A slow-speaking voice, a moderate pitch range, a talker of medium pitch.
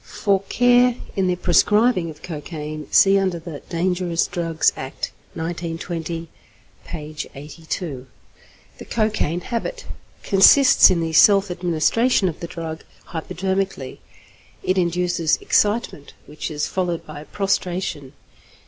Yes: slow, 115 wpm; average, 3.3 semitones; medium, 175 Hz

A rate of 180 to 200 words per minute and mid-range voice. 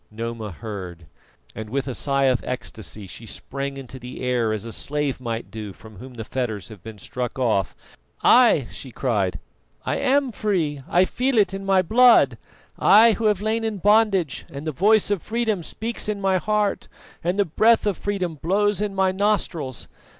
Yes: average, 185 wpm; medium, 155 Hz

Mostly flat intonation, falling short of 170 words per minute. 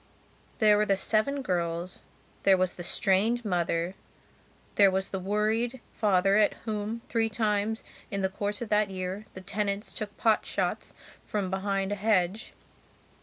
Yes: narrow, 2.2 semitones; average, 155 wpm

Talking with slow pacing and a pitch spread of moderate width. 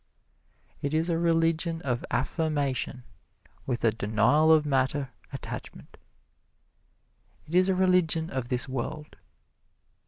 Yes: slow, 115 wpm; average, 4.2 semitones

